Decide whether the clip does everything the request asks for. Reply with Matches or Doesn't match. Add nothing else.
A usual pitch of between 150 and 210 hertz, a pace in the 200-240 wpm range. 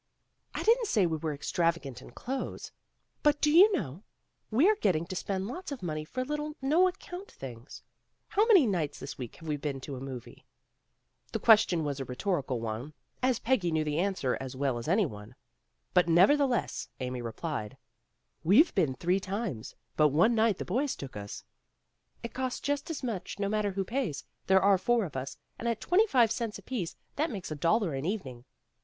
Matches